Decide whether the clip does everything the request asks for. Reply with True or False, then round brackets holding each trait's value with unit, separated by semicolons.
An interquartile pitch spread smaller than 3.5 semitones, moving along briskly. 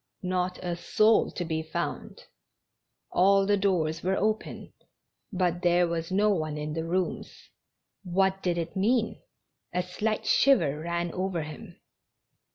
False (2.6 semitones; 140 wpm)